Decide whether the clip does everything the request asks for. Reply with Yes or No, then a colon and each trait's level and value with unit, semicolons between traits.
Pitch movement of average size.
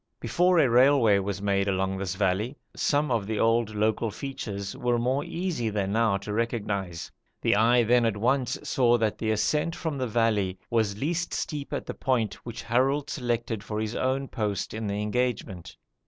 Yes: average, 4.0 semitones